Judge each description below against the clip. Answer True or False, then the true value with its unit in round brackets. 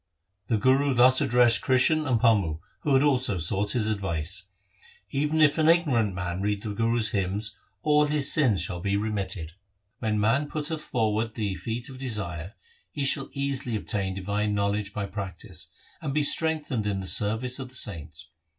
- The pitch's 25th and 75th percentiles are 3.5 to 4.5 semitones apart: False (5.2 semitones)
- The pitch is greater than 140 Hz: False (110 Hz)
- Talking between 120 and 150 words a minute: False (175 wpm)